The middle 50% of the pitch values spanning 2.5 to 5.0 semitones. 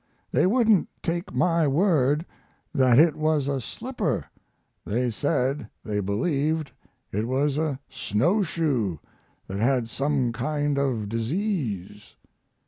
No: wide, 5.5 semitones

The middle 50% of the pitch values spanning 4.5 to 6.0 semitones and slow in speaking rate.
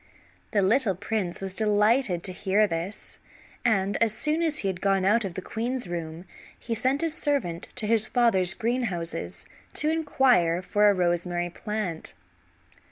No: average, 4.8 semitones; average, 160 wpm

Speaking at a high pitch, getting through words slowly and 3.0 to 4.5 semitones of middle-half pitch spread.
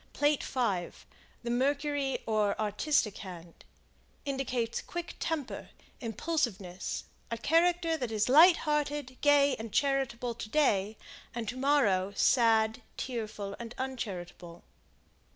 No: high, 245 Hz; slow, 115 wpm; average, 5.2 semitones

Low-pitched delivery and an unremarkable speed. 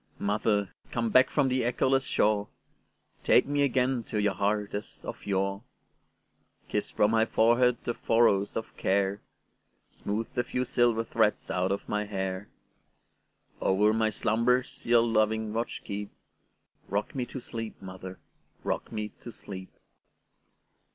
No: low, 110 Hz; slow, 125 wpm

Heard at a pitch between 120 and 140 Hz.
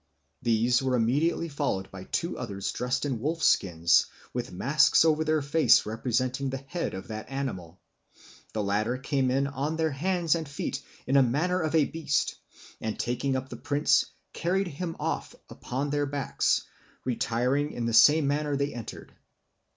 Yes: low, 135 Hz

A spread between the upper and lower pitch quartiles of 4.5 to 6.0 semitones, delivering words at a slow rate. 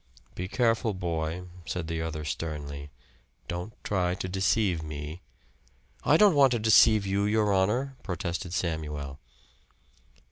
Yes: average, 5.2 semitones; slow, 130 wpm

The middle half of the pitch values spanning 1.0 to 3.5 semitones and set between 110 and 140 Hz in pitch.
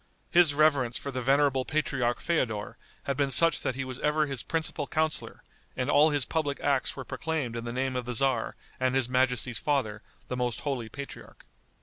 Yes: average, 2.8 semitones; low, 135 Hz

